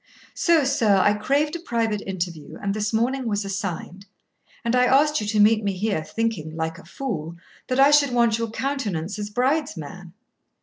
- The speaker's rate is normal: Yes, average, 185 wpm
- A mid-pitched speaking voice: No, high, 215 Hz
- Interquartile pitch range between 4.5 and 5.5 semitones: Yes, average, 5.2 semitones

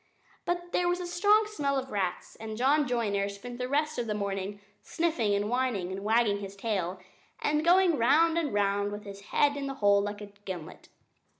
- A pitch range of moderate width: No, wide, 6.7 semitones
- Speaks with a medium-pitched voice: No, high, 230 Hz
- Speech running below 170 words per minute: No, average, 200 wpm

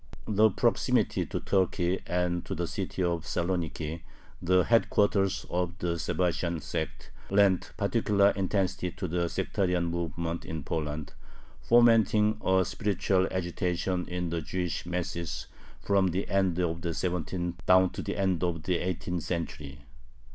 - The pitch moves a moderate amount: No, narrow, 1.9 semitones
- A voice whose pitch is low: Yes, very low, 90 Hz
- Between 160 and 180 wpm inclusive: No, average, 140 wpm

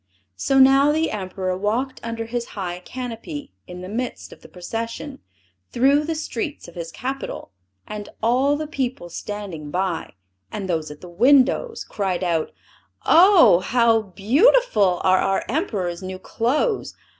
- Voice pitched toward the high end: Yes, high, 225 Hz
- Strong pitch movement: Yes, wide, 6.7 semitones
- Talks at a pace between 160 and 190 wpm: No, average, 145 wpm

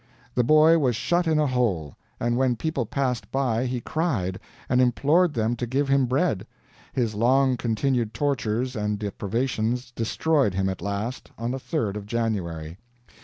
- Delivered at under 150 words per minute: No, average, 165 wpm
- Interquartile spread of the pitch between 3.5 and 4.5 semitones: Yes, average, 4.1 semitones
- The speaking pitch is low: Yes, low, 120 Hz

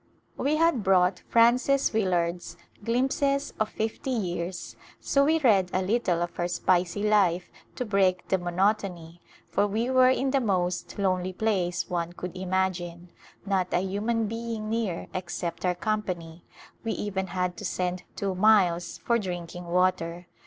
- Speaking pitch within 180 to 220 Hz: Yes, high, 190 Hz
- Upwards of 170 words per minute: No, average, 155 wpm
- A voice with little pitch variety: No, average, 3.8 semitones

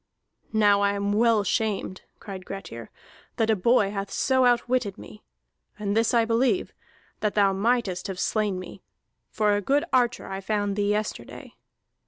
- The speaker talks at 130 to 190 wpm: Yes, average, 160 wpm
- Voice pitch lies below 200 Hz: No, high, 210 Hz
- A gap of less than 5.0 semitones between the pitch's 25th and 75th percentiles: Yes, narrow, 2.6 semitones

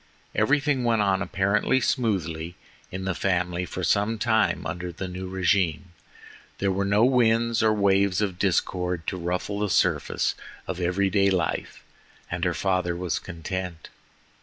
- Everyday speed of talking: Yes, average, 150 wpm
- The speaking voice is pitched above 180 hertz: No, very low, 95 Hz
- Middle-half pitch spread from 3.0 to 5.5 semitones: No, narrow, 2.5 semitones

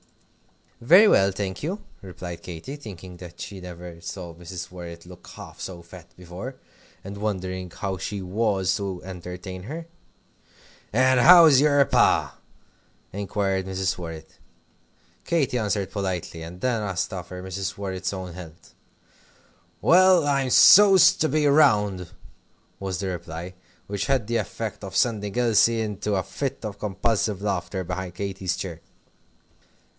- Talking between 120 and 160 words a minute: Yes, average, 140 wpm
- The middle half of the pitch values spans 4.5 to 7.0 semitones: No, average, 3.8 semitones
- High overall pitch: No, very low, 95 Hz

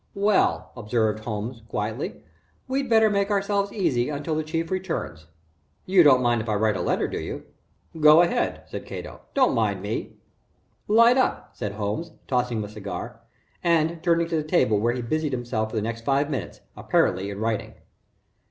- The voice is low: Yes, low, 125 Hz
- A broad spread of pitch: Yes, wide, 7.6 semitones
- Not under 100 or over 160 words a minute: No, average, 180 wpm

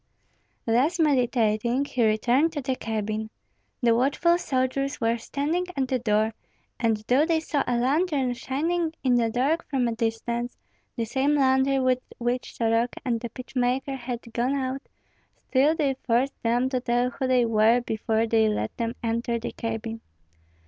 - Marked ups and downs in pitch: No, average, 3.0 semitones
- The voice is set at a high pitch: Yes, high, 245 Hz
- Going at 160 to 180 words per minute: Yes, average, 165 wpm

